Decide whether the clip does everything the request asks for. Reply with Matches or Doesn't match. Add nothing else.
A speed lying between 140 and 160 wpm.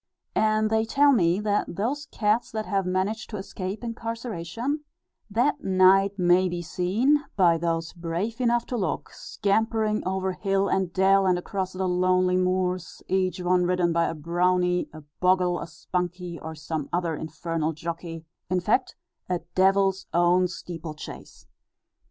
Matches